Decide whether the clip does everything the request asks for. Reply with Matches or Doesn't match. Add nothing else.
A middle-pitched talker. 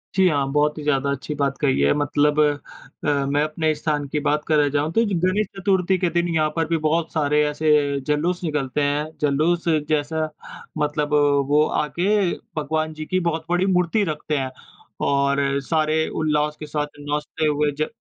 Matches